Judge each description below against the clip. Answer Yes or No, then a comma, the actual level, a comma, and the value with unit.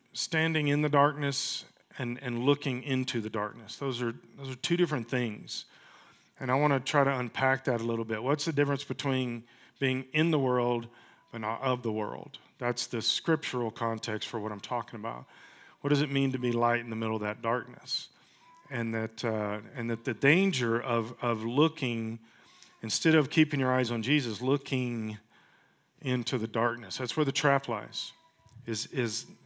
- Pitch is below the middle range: Yes, low, 125 Hz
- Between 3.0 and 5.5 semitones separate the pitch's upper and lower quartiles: Yes, average, 3.4 semitones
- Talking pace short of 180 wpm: No, average, 185 wpm